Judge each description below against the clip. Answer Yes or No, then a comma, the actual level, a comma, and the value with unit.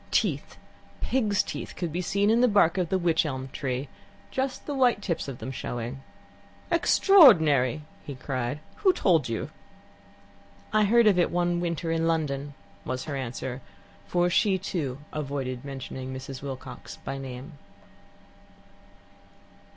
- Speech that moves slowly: No, average, 145 wpm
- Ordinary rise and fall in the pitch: No, wide, 6.1 semitones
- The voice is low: No, medium, 155 Hz